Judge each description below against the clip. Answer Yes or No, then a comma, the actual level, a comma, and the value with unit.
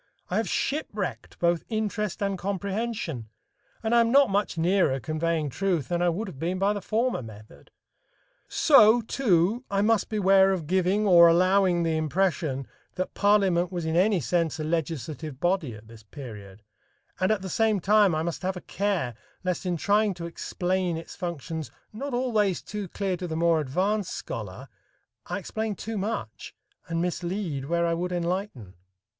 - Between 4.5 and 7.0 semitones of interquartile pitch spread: No, average, 3.9 semitones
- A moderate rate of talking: Yes, average, 170 wpm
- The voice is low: No, medium, 180 Hz